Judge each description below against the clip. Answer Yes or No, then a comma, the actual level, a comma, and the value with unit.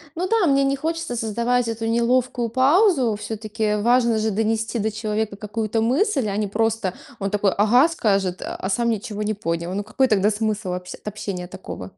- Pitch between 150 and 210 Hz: No, high, 220 Hz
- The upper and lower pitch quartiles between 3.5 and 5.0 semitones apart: No, average, 2.9 semitones